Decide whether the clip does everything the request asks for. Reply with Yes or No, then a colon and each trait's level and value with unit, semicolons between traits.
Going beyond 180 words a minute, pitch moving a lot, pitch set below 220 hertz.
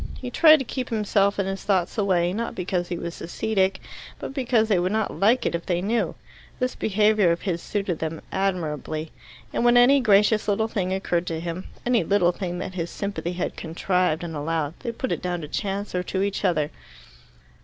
No: fast, 205 wpm; average, 3.8 semitones; high, 190 Hz